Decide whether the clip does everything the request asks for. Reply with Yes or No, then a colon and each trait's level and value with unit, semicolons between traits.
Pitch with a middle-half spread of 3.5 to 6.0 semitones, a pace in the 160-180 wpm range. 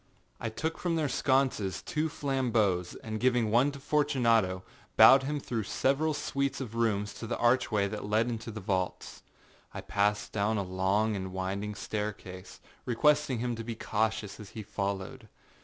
Yes: average, 4.5 semitones; average, 165 wpm